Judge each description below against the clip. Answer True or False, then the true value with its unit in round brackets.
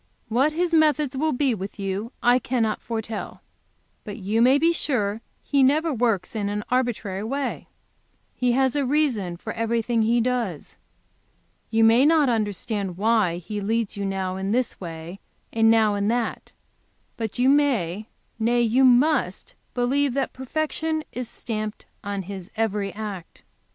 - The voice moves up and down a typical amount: True (4.3 semitones)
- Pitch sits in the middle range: False (230 Hz)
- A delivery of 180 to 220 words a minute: False (155 wpm)